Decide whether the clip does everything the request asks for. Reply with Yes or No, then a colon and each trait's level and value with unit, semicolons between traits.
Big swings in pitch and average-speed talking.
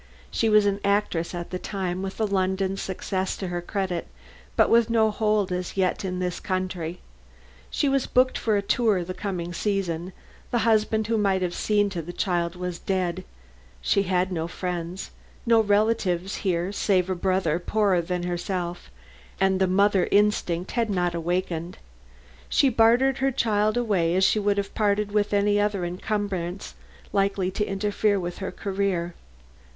No: narrow, 2.6 semitones; average, 165 wpm